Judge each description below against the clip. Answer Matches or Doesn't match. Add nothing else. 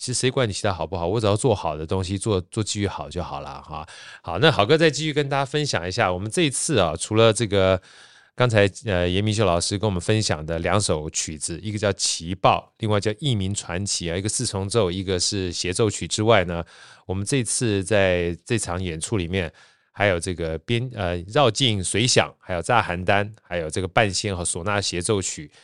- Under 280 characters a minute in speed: Doesn't match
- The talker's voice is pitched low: Matches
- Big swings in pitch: Doesn't match